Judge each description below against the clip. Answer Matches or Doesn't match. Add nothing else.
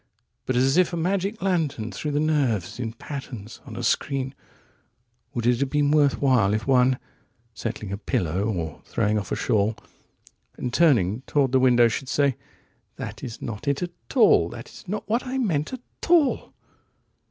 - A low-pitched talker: Matches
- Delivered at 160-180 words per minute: Matches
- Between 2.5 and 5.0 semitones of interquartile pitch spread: Doesn't match